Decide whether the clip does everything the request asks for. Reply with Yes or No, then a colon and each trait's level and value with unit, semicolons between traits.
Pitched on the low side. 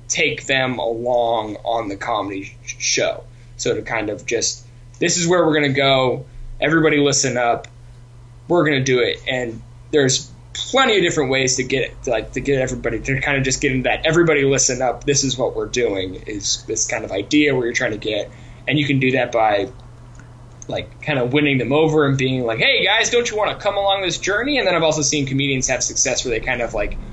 Yes: low, 130 Hz